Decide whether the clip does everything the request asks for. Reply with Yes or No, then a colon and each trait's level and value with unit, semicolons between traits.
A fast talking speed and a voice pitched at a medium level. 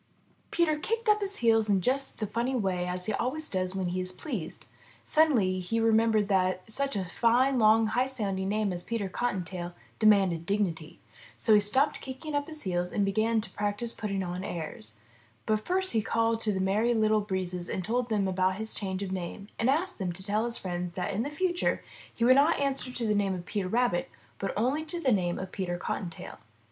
No: fast, 215 wpm; high, 210 Hz